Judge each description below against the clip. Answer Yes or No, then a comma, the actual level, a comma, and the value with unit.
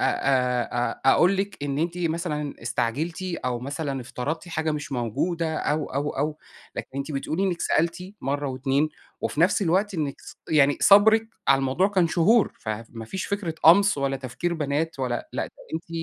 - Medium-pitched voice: Yes, medium, 150 Hz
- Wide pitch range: No, average, 4.3 semitones